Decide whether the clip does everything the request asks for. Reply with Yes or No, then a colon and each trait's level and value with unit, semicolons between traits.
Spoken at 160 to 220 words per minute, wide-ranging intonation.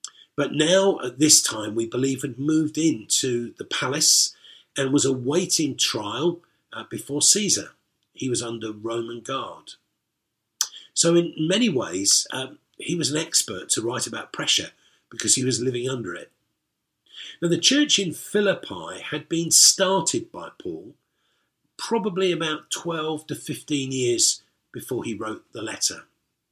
No: average, 140 wpm; wide, 6.5 semitones